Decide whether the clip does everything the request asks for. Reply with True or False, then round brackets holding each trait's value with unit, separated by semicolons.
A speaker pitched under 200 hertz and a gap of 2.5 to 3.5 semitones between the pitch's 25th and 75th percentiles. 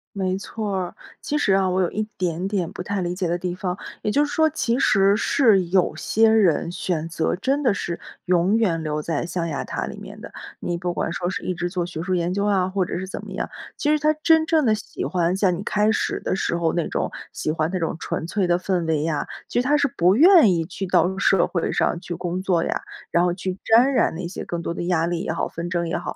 True (185 Hz; 3.0 semitones)